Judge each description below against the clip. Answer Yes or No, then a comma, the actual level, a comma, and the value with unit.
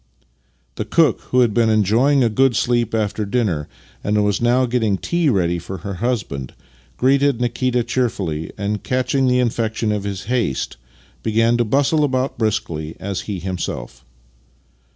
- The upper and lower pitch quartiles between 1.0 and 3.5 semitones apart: No, average, 4.0 semitones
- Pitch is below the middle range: Yes, low, 115 Hz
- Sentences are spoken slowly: No, average, 155 wpm